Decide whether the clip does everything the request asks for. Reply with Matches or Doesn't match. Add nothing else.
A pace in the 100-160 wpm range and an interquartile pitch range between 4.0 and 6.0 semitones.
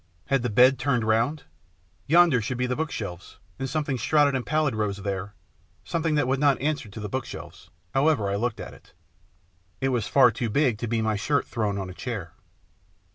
Doesn't match